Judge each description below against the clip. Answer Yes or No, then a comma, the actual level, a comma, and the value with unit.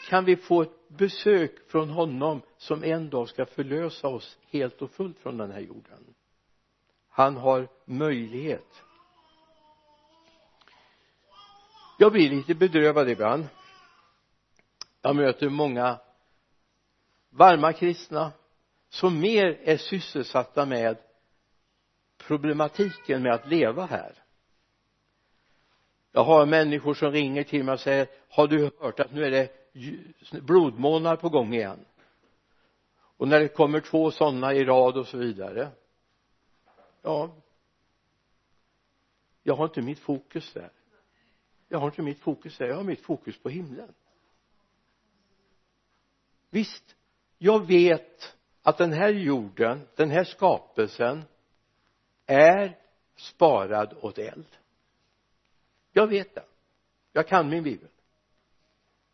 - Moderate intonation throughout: Yes, average, 4.5 semitones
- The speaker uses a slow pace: Yes, slow, 115 wpm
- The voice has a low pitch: No, medium, 150 Hz